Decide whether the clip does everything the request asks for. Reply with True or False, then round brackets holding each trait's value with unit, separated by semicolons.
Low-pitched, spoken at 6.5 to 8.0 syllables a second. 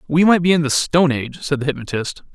False (150 Hz; 6.6 syllables/s)